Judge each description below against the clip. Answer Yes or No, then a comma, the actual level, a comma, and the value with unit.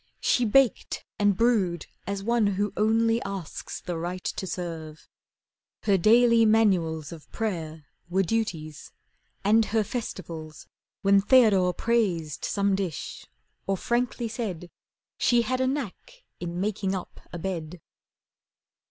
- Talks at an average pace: No, slow, 125 wpm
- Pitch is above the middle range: Yes, high, 195 Hz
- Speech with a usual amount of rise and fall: Yes, average, 4.6 semitones